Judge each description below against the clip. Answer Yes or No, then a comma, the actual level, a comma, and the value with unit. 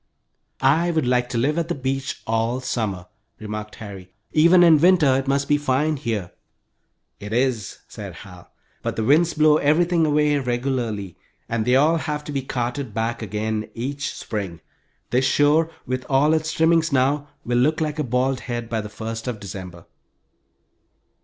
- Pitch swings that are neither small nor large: Yes, average, 4.9 semitones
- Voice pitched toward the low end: Yes, low, 130 Hz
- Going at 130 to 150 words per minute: No, average, 170 wpm